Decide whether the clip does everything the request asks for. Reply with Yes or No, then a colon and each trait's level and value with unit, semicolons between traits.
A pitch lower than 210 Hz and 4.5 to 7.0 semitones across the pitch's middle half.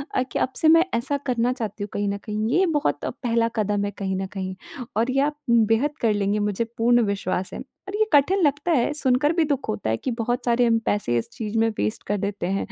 No: high, 230 Hz; average, 5.0 semitones